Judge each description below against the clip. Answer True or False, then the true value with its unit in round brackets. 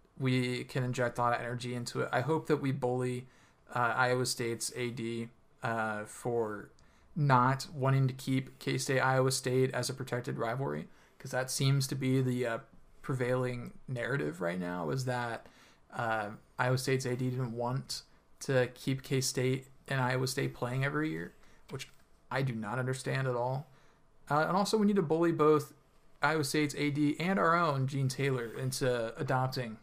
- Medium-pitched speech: False (130 Hz)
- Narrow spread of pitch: True (1.9 semitones)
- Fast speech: False (170 wpm)